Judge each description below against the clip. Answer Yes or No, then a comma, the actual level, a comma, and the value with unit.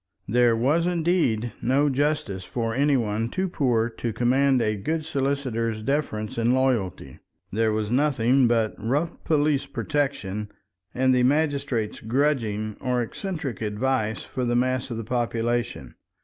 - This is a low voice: Yes, low, 125 Hz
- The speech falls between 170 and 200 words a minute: No, average, 140 wpm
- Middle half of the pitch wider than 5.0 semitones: No, average, 3.9 semitones